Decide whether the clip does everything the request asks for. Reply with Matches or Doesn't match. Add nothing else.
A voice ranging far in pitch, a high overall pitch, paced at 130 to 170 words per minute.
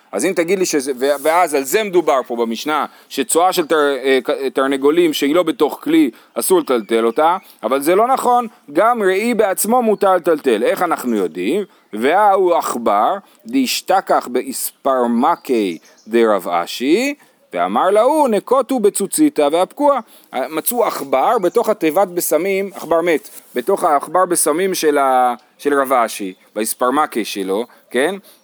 Doesn't match